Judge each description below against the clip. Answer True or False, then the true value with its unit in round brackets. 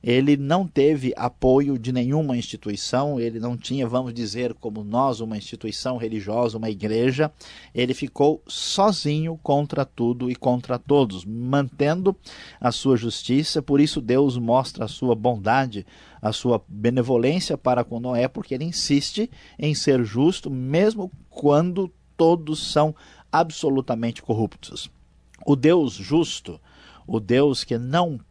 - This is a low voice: True (130 Hz)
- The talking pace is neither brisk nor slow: True (135 wpm)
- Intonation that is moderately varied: True (3.8 semitones)